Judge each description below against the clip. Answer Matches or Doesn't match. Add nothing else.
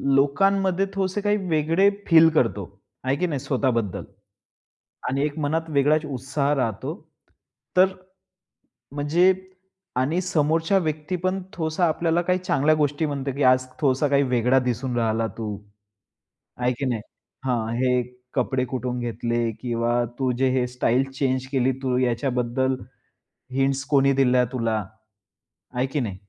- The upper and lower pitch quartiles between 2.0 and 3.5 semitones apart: Doesn't match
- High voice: Doesn't match